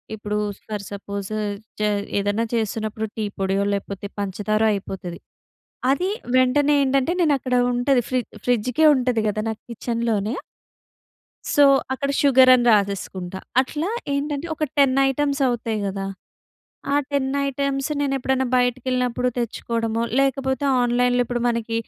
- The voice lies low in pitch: No, high, 245 Hz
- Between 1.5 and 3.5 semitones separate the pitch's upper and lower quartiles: No, average, 4.1 semitones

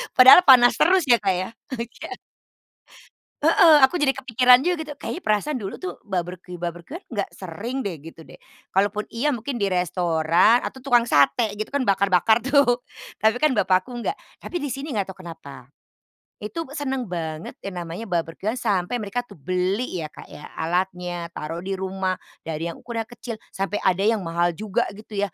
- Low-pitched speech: No, high, 205 Hz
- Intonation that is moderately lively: No, wide, 5.9 semitones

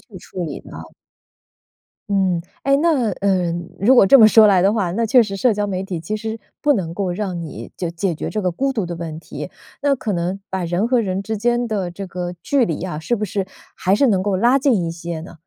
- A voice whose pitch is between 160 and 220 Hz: Yes, high, 195 Hz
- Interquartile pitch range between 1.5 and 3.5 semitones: No, average, 4.2 semitones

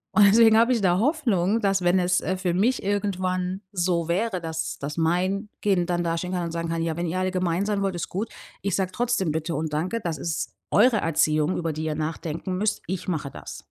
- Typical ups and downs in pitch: Yes, average, 3.0 semitones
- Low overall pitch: No, medium, 180 Hz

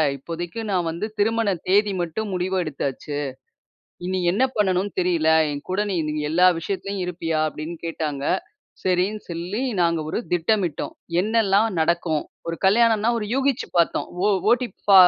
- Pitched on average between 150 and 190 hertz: Yes, medium, 185 Hz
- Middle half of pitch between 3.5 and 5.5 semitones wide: Yes, average, 3.8 semitones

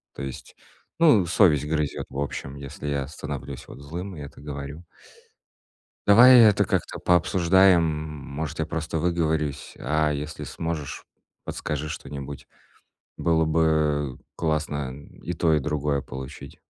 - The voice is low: Yes, very low, 75 Hz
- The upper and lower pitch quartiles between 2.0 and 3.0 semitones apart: Yes, narrow, 2.6 semitones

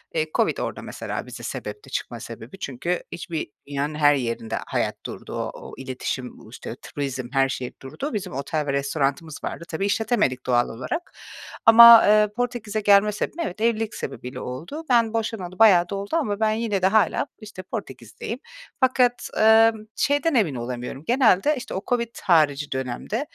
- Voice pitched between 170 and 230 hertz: Yes, high, 190 Hz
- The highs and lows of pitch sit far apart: Yes, wide, 8.5 semitones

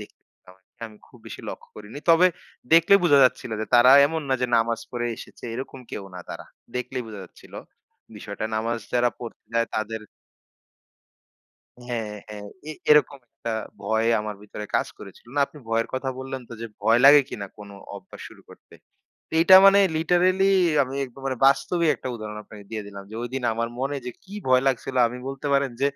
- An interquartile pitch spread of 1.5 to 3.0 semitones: No, average, 4.0 semitones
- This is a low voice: Yes, low, 125 Hz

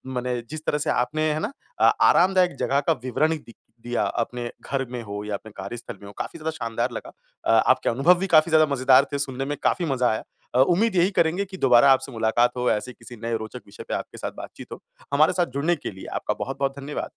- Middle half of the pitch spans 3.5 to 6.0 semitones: Yes, average, 4.6 semitones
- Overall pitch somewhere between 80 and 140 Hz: Yes, low, 135 Hz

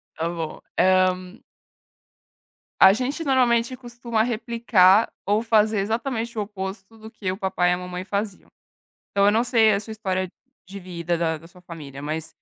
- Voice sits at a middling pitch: No, high, 200 Hz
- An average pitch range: Yes, average, 4.0 semitones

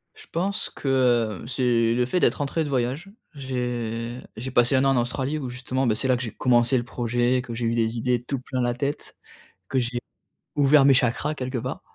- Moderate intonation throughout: No, narrow, 2.0 semitones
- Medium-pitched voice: No, low, 125 Hz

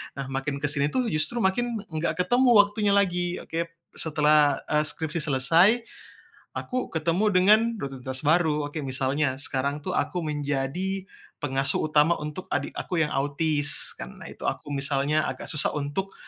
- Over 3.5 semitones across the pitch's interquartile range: Yes, average, 4.2 semitones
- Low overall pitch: No, medium, 155 Hz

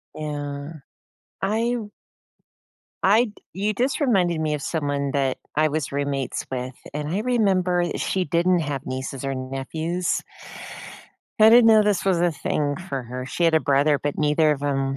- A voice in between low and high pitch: Yes, medium, 155 Hz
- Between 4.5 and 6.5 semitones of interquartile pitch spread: Yes, average, 5.0 semitones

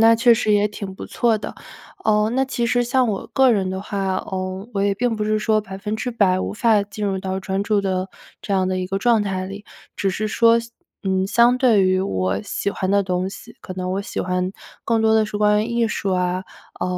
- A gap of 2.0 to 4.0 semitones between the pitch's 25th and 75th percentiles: Yes, average, 2.8 semitones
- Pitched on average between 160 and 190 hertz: No, high, 205 Hz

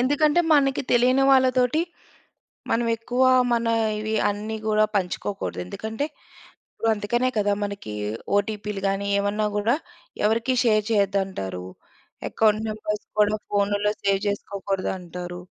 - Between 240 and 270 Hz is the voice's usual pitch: No, high, 210 Hz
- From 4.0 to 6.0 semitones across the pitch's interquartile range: No, average, 2.8 semitones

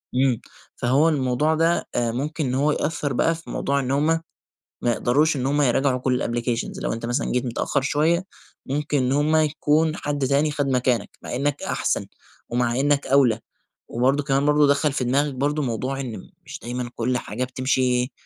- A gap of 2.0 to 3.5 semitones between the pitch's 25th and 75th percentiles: Yes, average, 2.8 semitones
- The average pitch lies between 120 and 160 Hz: Yes, low, 135 Hz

